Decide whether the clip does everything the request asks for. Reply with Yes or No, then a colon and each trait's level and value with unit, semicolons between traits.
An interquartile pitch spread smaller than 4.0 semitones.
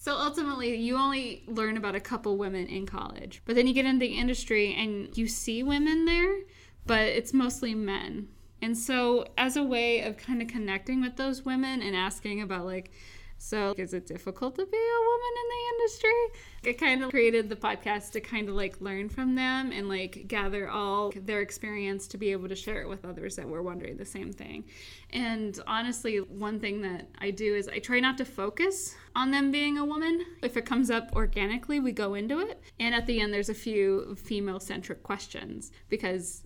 No: average, 4.6 semitones